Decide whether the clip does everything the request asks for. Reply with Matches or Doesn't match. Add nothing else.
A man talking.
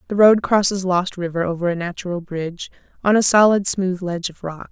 Doesn't match